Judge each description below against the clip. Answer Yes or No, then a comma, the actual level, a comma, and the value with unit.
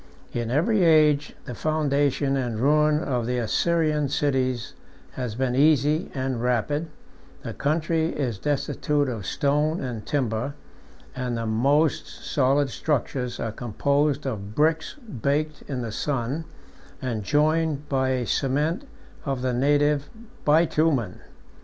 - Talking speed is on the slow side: Yes, slow, 130 wpm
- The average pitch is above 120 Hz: Yes, medium, 140 Hz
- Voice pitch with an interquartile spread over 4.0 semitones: No, average, 3.3 semitones